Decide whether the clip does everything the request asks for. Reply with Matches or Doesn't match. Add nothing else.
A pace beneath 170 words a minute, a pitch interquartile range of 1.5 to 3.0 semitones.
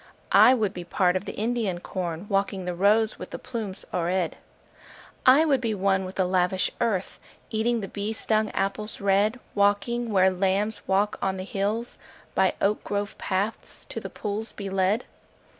Doesn't match